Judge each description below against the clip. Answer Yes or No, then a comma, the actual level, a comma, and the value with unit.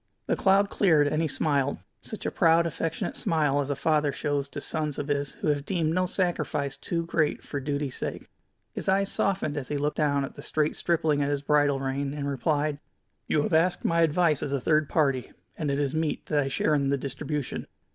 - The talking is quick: Yes, fast, 215 wpm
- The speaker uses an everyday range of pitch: No, narrow, 2.3 semitones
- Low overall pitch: No, medium, 150 Hz